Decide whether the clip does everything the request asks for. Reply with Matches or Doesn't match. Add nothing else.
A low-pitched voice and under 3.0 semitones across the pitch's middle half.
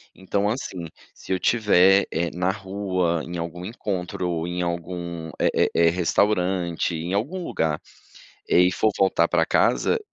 Matches